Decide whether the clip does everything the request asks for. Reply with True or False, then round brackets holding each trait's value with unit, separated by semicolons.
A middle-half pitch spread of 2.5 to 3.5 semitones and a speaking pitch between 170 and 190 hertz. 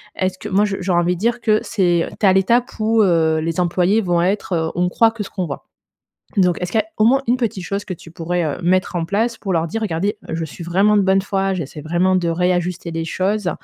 True (3.2 semitones; 185 Hz)